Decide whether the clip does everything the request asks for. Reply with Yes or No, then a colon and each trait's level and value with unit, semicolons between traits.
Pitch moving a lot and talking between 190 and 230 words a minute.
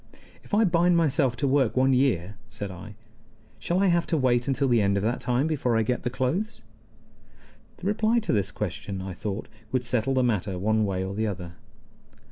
Yes: wide, 5.8 semitones; fast, 205 wpm